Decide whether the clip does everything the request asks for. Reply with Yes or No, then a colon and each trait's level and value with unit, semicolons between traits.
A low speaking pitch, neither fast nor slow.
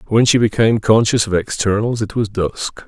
Yes: low, 110 Hz; average, 190 wpm